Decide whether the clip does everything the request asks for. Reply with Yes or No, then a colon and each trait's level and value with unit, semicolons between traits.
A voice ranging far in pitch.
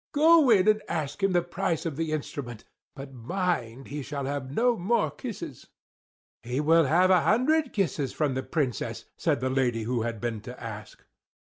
Yes: wide, 6.9 semitones